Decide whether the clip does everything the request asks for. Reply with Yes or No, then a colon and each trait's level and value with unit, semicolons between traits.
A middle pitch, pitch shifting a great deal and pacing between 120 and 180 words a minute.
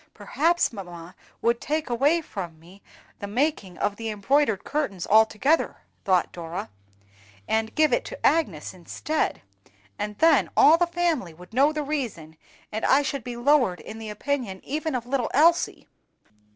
No: high, 240 Hz; wide, 7.4 semitones; average, 155 wpm